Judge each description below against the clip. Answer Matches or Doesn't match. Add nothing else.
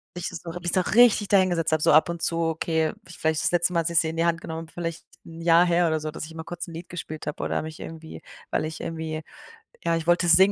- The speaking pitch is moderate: Matches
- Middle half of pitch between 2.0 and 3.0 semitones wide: Doesn't match